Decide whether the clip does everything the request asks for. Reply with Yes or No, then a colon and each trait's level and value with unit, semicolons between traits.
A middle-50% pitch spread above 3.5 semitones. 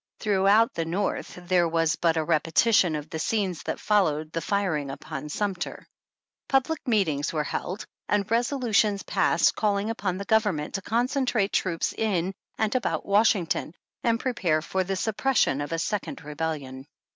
Yes: average, 5.1 semitones